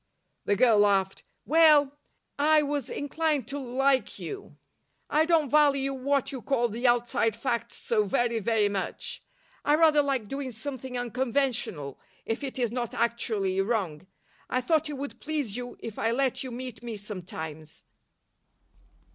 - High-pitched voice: Yes, very high, 250 Hz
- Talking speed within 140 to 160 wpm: Yes, average, 150 wpm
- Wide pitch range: No, average, 4.2 semitones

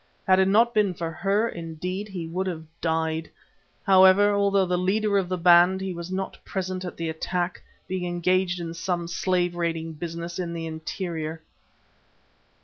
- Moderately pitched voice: Yes, medium, 180 Hz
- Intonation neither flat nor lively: No, narrow, 2.2 semitones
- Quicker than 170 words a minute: No, average, 165 wpm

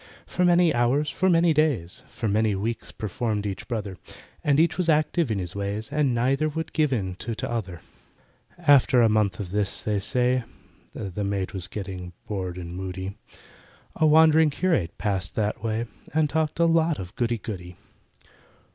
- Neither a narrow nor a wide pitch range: No, wide, 7.5 semitones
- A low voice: Yes, low, 115 Hz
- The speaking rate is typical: Yes, average, 165 wpm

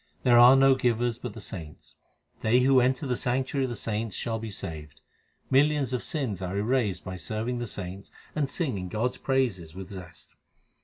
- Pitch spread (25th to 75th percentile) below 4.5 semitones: No, average, 5.0 semitones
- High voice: No, low, 115 Hz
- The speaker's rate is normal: Yes, average, 190 wpm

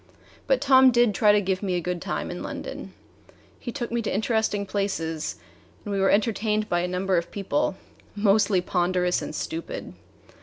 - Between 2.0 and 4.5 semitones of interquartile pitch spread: Yes, average, 3.5 semitones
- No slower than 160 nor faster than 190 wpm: Yes, average, 180 wpm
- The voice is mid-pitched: No, high, 200 Hz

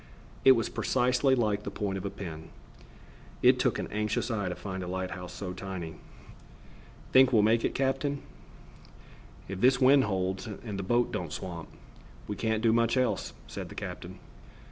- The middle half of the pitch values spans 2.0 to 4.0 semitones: No, average, 4.6 semitones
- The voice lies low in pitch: Yes, low, 105 Hz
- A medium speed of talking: Yes, average, 175 wpm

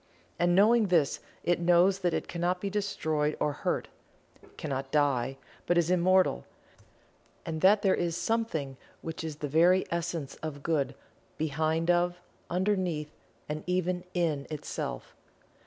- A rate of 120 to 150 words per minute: Yes, average, 140 wpm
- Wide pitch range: No, average, 3.3 semitones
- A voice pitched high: No, medium, 170 Hz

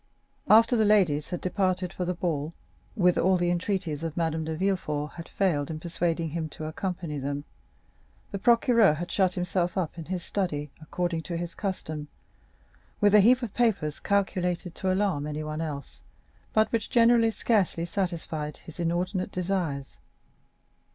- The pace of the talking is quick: No, average, 160 wpm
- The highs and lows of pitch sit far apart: No, average, 3.7 semitones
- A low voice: No, medium, 175 Hz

